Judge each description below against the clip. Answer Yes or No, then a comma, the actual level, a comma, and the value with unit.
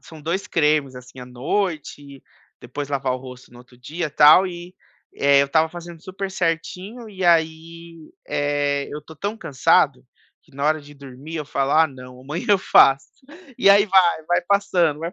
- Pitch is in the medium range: Yes, medium, 155 Hz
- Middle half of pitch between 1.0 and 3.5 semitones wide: No, average, 3.9 semitones